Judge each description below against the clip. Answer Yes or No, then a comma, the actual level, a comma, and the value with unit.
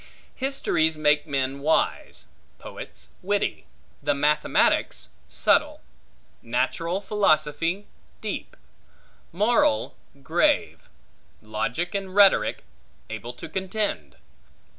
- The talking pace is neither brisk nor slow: No, slow, 80 wpm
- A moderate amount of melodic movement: No, wide, 6.4 semitones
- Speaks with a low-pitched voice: No, medium, 160 Hz